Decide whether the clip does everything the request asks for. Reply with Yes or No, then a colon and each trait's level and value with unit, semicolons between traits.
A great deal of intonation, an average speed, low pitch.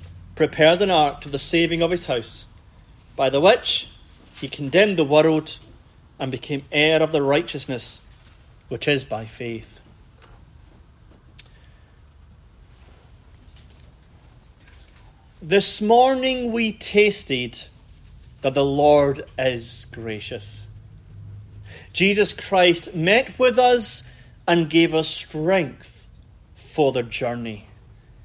No: wide, 7.1 semitones; slow, 100 wpm; low, 130 Hz